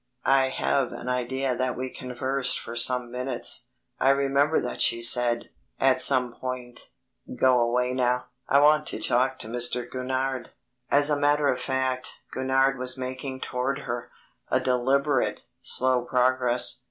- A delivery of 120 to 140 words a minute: No, average, 150 wpm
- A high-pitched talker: No, low, 130 Hz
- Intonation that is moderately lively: No, narrow, 1.3 semitones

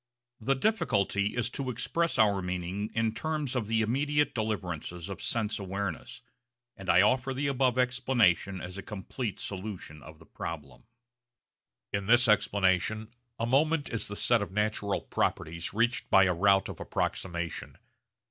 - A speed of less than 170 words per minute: Yes, average, 150 wpm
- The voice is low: Yes, low, 105 Hz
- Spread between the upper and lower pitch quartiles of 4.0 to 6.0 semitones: Yes, average, 4.7 semitones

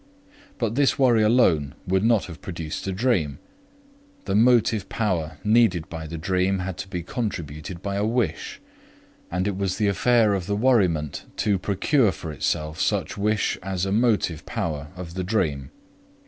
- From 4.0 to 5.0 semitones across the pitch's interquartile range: Yes, average, 4.5 semitones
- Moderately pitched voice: No, very low, 95 Hz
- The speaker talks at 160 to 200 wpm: Yes, average, 165 wpm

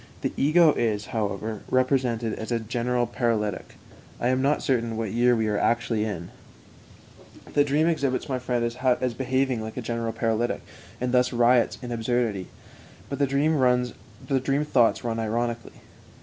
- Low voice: Yes, low, 120 Hz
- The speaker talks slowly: No, average, 150 wpm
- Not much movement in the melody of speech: Yes, narrow, 2.3 semitones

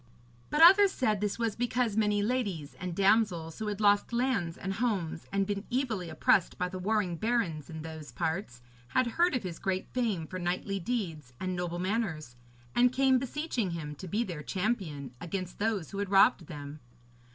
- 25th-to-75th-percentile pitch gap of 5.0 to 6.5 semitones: Yes, wide, 5.4 semitones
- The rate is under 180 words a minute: No, average, 185 wpm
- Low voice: No, high, 195 Hz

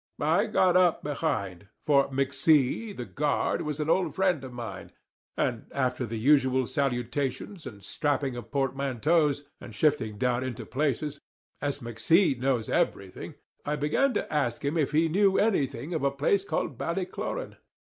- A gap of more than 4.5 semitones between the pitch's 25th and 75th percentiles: No, average, 4.0 semitones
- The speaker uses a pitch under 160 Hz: Yes, medium, 140 Hz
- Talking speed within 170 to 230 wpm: No, average, 155 wpm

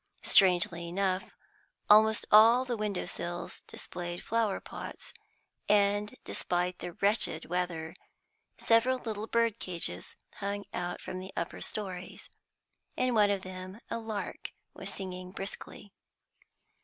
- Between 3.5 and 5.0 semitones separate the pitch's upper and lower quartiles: No, average, 3.1 semitones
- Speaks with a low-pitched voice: No, high, 195 Hz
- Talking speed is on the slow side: Yes, slow, 120 wpm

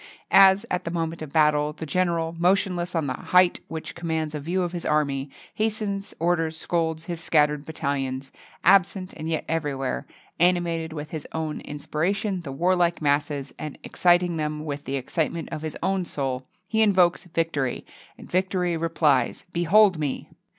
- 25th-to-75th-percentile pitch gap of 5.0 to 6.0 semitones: No, average, 3.0 semitones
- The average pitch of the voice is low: No, medium, 165 Hz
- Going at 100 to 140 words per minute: No, average, 160 wpm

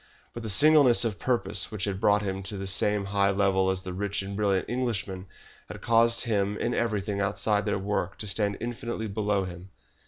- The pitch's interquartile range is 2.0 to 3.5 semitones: Yes, narrow, 2.4 semitones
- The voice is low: Yes, low, 100 Hz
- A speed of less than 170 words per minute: No, average, 195 wpm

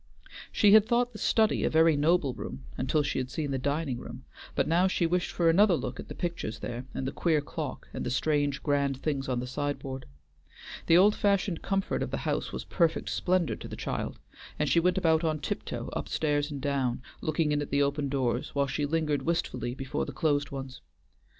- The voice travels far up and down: No, average, 3.7 semitones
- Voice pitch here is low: No, medium, 150 Hz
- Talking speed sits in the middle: No, fast, 215 wpm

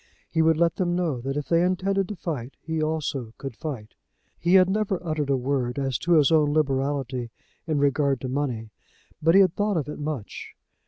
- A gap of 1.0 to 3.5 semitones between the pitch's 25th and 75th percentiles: No, average, 4.0 semitones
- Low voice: No, medium, 150 Hz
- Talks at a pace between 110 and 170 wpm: No, fast, 205 wpm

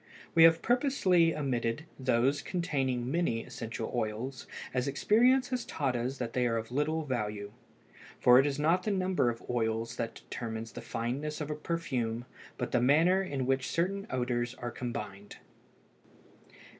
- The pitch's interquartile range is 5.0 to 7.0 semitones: Yes, wide, 5.6 semitones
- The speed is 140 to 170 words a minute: Yes, average, 155 wpm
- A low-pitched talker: Yes, low, 130 Hz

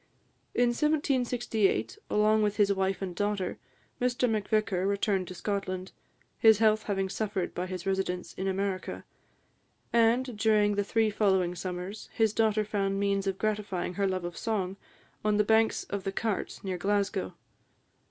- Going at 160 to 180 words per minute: No, average, 150 wpm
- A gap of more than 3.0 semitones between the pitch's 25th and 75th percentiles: No, narrow, 2.4 semitones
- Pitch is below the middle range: No, high, 200 Hz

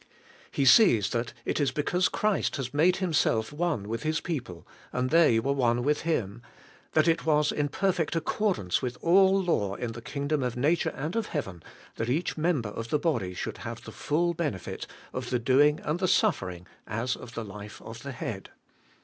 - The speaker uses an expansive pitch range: Yes, wide, 6.2 semitones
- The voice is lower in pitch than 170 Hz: Yes, medium, 140 Hz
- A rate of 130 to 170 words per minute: No, average, 190 wpm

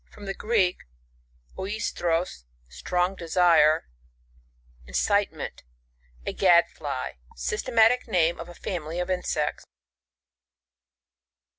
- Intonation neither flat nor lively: Yes, average, 3.2 semitones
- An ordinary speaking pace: No, slow, 100 wpm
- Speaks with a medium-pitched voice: Yes, medium, 175 Hz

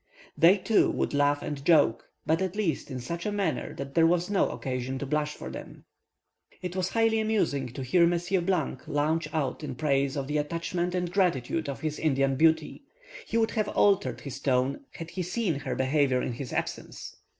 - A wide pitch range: No, average, 4.6 semitones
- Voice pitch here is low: No, medium, 155 Hz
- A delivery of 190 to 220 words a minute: Yes, average, 195 wpm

